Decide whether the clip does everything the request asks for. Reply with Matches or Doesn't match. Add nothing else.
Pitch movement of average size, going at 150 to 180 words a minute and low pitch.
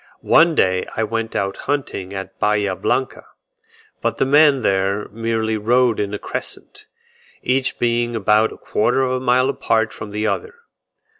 Matches